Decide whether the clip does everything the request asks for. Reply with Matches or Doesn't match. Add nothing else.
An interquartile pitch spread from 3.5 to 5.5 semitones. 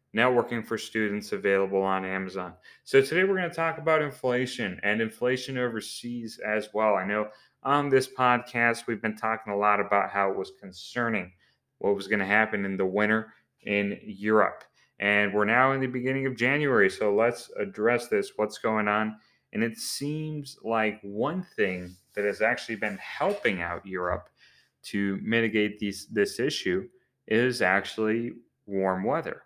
Matches